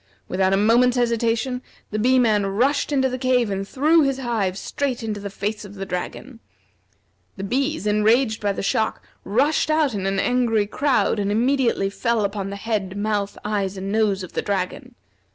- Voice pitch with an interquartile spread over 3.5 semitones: Yes, average, 4.0 semitones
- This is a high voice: Yes, high, 220 Hz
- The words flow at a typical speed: Yes, average, 185 wpm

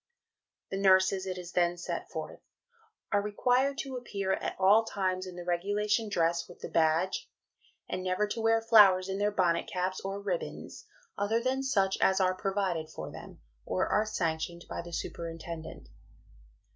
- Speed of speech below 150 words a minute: No, average, 165 wpm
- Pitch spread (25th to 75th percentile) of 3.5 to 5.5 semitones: No, average, 3.1 semitones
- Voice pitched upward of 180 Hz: Yes, high, 190 Hz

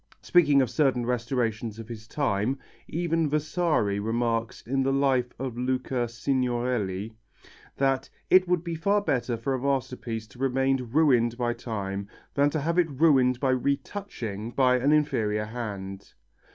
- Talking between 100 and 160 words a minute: Yes, average, 150 wpm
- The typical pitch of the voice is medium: No, low, 125 Hz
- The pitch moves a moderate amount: Yes, average, 3.6 semitones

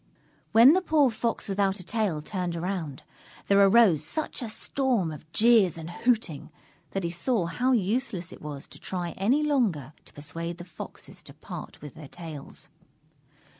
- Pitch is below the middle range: No, high, 190 Hz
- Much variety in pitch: Yes, wide, 6.0 semitones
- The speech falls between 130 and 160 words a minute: No, average, 170 wpm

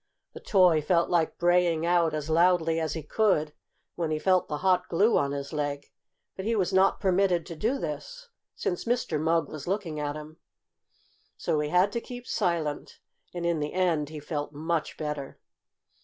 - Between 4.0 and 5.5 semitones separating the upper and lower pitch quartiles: No, average, 3.3 semitones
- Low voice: No, medium, 165 Hz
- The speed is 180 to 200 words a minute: Yes, average, 185 wpm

